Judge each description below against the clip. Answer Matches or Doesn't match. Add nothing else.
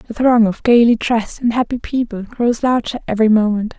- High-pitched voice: Matches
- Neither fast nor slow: Matches